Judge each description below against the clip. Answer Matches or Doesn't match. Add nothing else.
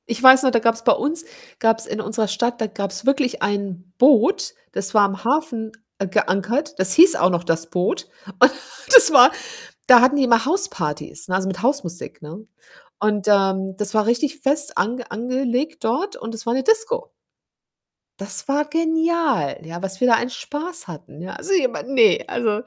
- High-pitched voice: Matches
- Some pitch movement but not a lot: Doesn't match